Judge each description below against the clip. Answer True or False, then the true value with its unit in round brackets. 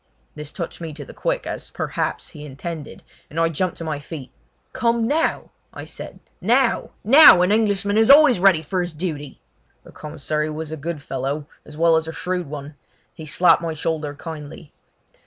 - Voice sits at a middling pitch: True (165 Hz)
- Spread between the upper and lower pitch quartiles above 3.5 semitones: True (4.0 semitones)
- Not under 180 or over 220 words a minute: True (185 wpm)